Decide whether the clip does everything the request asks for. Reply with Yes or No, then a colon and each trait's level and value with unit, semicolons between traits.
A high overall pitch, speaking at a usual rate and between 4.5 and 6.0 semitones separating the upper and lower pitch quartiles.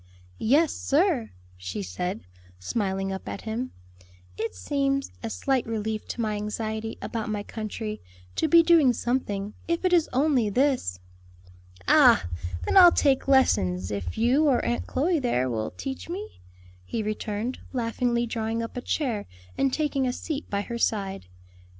Yes: high, 235 Hz; average, 155 wpm; average, 4.8 semitones